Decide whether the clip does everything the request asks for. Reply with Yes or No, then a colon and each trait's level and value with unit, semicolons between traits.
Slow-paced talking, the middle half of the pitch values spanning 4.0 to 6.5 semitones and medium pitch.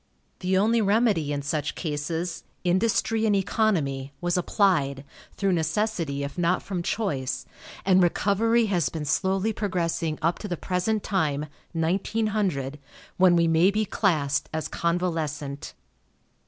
Yes: slow, 130 wpm; average, 4.8 semitones; medium, 175 Hz